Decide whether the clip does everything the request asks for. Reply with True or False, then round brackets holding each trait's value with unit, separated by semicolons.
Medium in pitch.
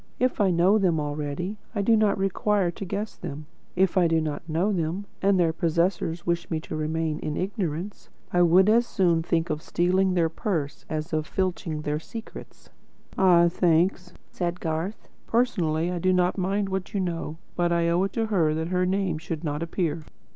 True (175 Hz)